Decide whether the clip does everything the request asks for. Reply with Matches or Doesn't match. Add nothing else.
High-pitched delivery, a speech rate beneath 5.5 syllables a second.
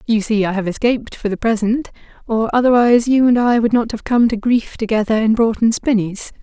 Doesn't match